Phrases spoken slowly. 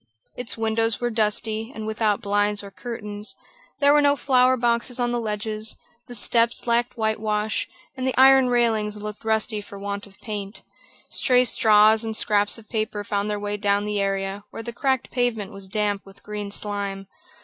No: average, 180 wpm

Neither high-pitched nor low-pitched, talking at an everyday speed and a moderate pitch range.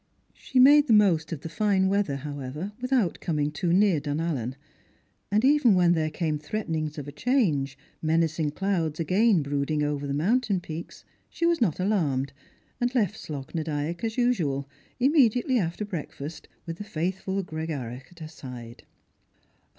No: medium, 165 Hz; average, 160 wpm; wide, 6.0 semitones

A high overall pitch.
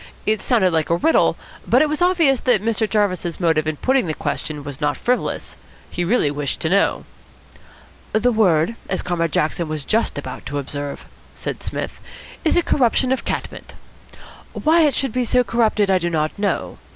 Yes: high, 200 Hz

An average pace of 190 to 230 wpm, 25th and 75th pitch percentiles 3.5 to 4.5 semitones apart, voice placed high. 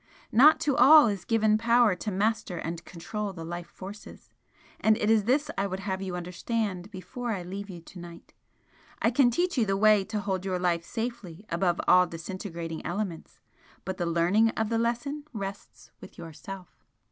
No: average, 180 wpm; average, 4.2 semitones; high, 195 Hz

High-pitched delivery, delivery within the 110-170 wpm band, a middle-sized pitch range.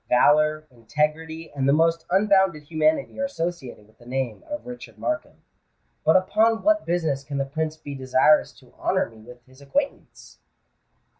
No: medium, 155 Hz; average, 160 wpm; average, 4.6 semitones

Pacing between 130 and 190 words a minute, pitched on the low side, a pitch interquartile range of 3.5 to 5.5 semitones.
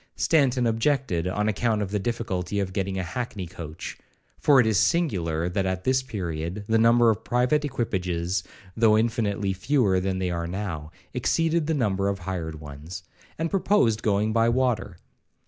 Yes: average, 165 wpm; low, 105 Hz; average, 4.7 semitones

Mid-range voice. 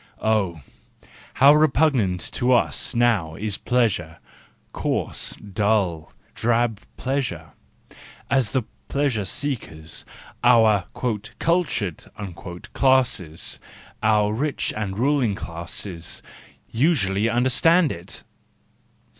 No: low, 110 Hz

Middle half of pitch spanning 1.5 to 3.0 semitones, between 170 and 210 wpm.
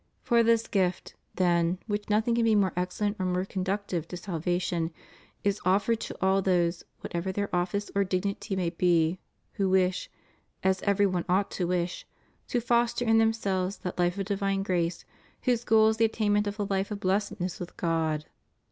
Yes: narrow, 2.5 semitones; average, 185 wpm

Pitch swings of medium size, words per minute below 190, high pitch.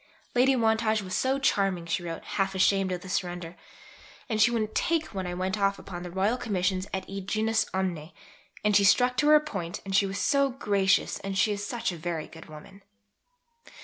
No: average, 3.2 semitones; average, 200 wpm; high, 195 Hz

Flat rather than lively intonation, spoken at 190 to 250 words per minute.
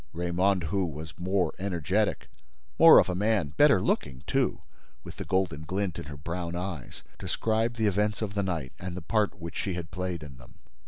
No: average, 3.2 semitones; average, 195 wpm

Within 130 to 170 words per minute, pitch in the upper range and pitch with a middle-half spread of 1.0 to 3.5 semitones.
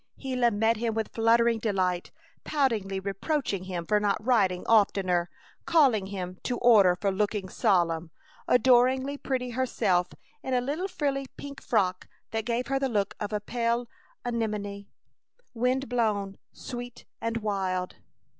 No: average, 145 wpm; high, 225 Hz; average, 4.0 semitones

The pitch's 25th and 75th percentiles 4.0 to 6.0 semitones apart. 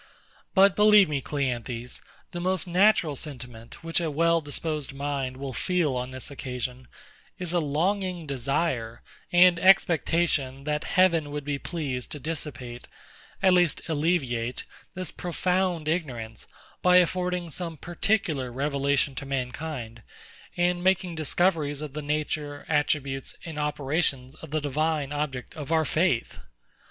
Yes: average, 4.3 semitones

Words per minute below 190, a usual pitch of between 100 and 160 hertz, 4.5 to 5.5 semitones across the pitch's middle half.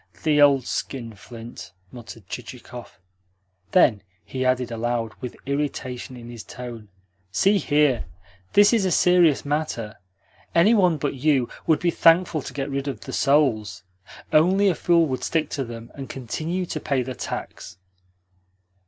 Yes: average, 150 wpm; low, 135 Hz; average, 5.0 semitones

